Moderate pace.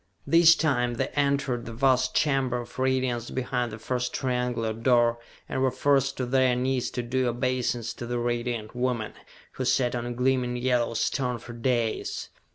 Yes: average, 170 wpm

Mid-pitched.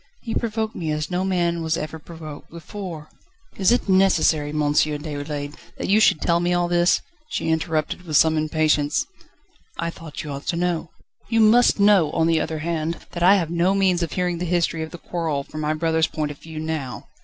Yes: medium, 165 Hz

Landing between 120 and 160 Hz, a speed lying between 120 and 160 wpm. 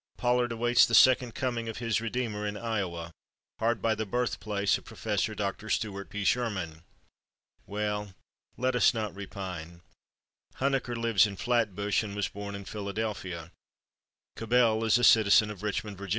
No: low, 105 Hz; average, 150 wpm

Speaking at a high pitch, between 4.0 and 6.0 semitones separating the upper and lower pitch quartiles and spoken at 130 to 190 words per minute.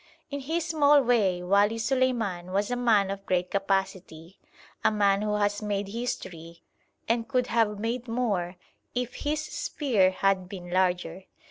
Yes: high, 205 Hz; average, 4.5 semitones; average, 150 wpm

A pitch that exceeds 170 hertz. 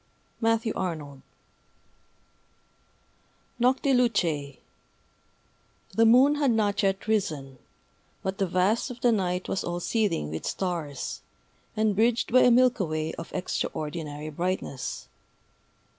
Yes: high, 190 Hz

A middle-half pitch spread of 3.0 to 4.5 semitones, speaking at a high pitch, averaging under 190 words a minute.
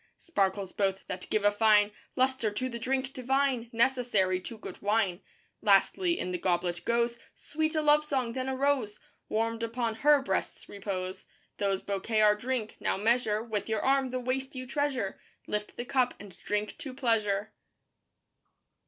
Yes: average, 4.1 semitones; high, 230 Hz; average, 165 wpm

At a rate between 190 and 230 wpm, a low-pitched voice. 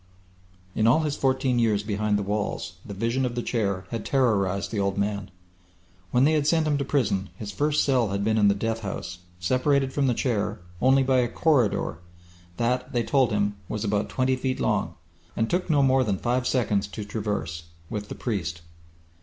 Yes: average, 195 wpm; low, 115 Hz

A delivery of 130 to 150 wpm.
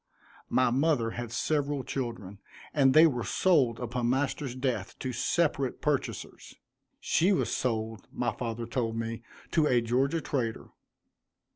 Yes: slow, 135 wpm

